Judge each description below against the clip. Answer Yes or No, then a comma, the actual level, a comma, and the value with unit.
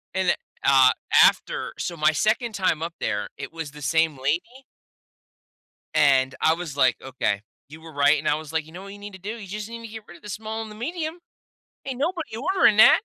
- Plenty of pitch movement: Yes, wide, 6.7 semitones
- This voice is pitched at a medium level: Yes, medium, 180 Hz